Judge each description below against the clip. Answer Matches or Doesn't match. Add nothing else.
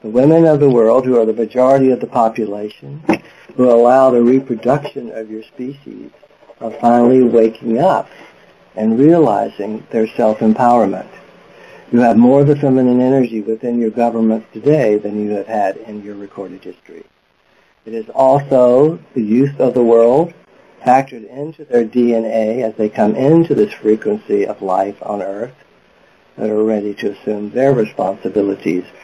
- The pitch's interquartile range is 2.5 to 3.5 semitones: Matches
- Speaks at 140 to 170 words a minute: Matches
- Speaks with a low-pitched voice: Matches